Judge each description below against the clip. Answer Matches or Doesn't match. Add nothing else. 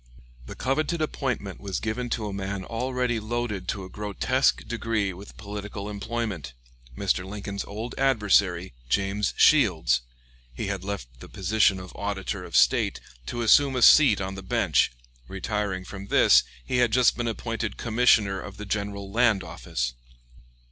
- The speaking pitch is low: Matches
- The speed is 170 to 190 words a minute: Doesn't match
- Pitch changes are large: Doesn't match